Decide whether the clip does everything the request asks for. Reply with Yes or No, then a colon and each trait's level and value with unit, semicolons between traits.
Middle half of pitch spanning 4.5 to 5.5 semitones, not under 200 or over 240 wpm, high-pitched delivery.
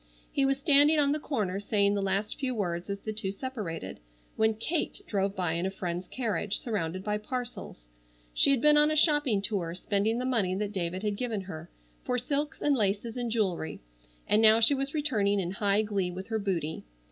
Yes: average, 4.9 semitones; fast, 205 wpm; high, 210 Hz